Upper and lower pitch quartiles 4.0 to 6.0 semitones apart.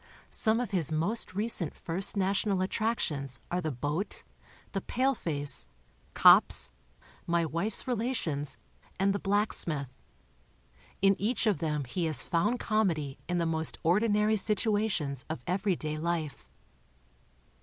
Yes: average, 5.2 semitones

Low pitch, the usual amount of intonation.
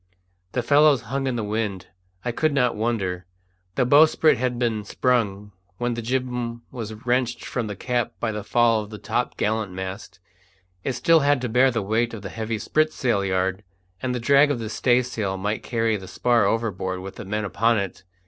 Yes: low, 115 Hz; average, 3.2 semitones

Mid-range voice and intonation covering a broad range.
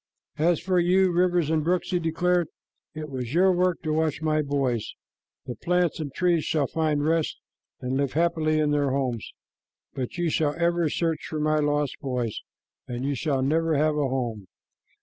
No: medium, 155 Hz; average, 3.4 semitones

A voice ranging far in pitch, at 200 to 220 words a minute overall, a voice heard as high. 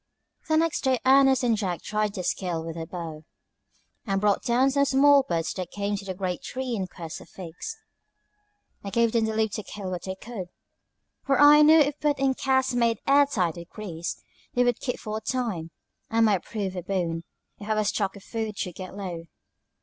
Yes: wide, 6.0 semitones; fast, 205 wpm; high, 215 Hz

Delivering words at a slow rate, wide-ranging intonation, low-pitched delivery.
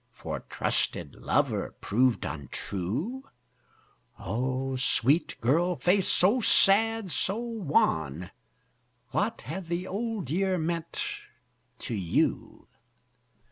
No: slow, 95 wpm; wide, 8.1 semitones; medium, 170 Hz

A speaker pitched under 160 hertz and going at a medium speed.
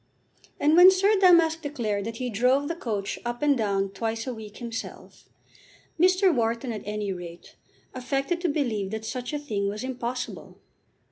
No: high, 245 Hz; average, 165 wpm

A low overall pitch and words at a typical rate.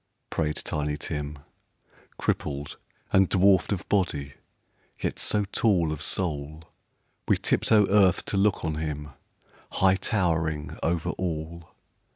No: very low, 80 Hz; slow, 125 wpm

